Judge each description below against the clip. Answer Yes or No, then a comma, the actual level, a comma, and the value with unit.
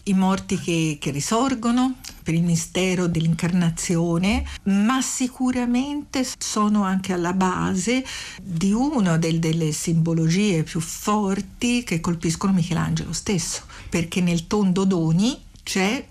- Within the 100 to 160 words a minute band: Yes, slow, 115 wpm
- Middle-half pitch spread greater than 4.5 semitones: No, average, 4.0 semitones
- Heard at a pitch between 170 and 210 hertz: Yes, medium, 185 Hz